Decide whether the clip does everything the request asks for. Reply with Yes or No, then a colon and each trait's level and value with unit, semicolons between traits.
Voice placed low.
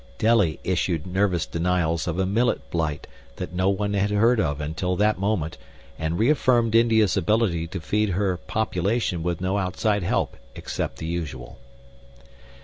Yes: very low, 95 Hz